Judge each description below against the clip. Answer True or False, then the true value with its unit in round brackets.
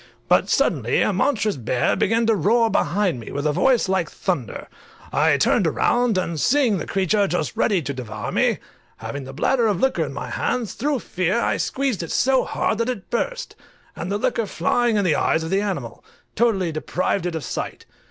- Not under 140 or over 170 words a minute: False (200 wpm)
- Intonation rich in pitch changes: True (6.4 semitones)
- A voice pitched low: False (200 Hz)